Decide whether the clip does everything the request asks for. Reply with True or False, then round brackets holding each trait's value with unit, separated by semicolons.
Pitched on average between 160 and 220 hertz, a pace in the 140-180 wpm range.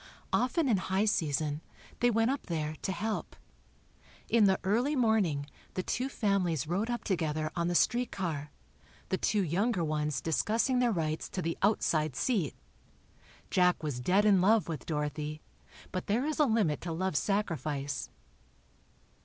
True (185 Hz; 155 wpm)